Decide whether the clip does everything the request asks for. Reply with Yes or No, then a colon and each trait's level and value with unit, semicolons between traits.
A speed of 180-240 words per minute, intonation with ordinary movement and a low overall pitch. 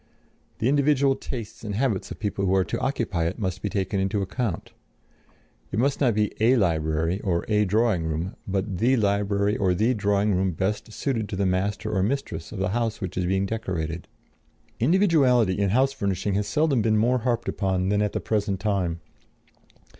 Yes: average, 190 wpm; average, 3.5 semitones; low, 105 Hz